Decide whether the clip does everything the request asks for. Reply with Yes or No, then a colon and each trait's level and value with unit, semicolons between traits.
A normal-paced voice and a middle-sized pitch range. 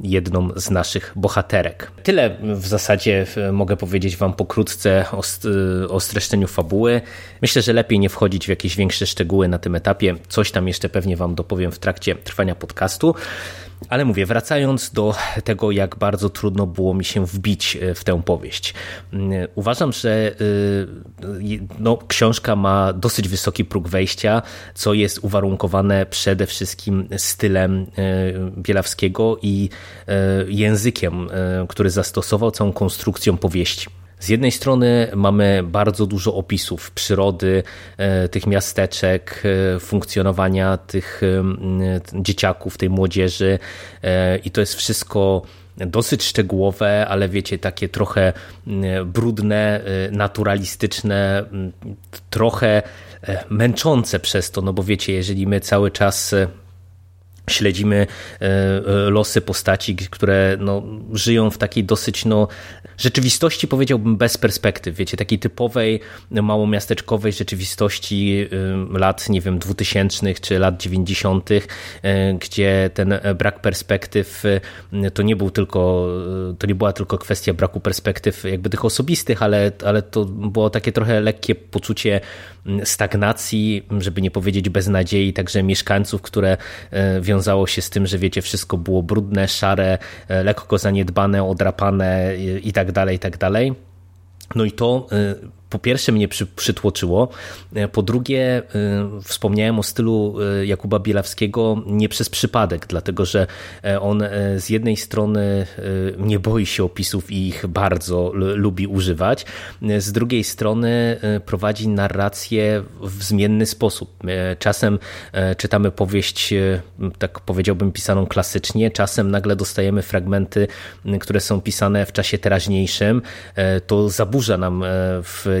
No: average, 125 wpm; narrow, 1.9 semitones